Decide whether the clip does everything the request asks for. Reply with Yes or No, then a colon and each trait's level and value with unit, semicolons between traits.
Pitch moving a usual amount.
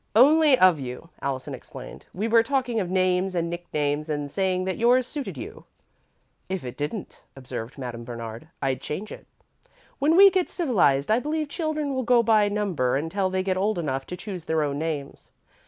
No: wide, 8.2 semitones